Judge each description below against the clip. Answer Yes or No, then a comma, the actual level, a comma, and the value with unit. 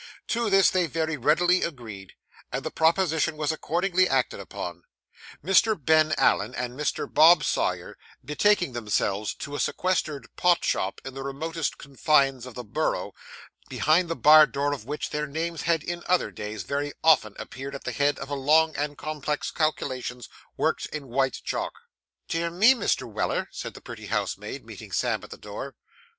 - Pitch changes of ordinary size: Yes, average, 3.9 semitones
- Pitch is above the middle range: No, medium, 150 Hz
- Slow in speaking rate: No, average, 170 wpm